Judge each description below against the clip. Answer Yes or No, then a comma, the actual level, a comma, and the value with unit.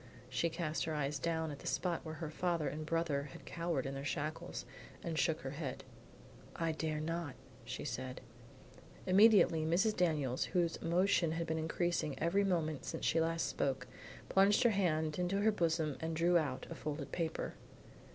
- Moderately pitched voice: Yes, medium, 160 Hz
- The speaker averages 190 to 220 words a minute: No, average, 175 wpm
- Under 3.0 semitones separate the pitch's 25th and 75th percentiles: Yes, narrow, 2.4 semitones